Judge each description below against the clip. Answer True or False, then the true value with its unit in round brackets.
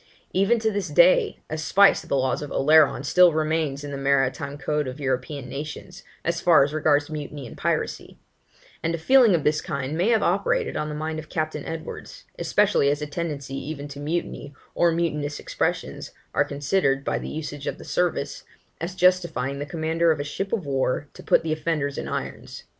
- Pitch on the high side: False (155 Hz)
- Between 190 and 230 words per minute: True (195 wpm)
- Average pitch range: True (3.2 semitones)